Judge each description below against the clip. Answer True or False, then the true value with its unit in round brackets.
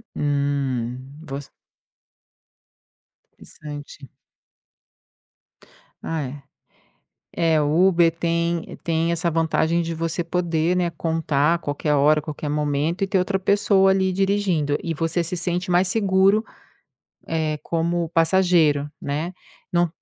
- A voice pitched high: False (165 Hz)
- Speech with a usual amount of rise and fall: True (3.0 semitones)